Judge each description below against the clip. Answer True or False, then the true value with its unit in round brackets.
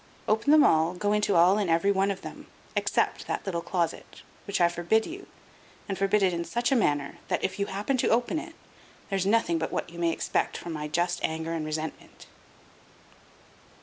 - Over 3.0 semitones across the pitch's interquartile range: True (3.9 semitones)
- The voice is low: False (190 Hz)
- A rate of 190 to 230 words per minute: True (200 wpm)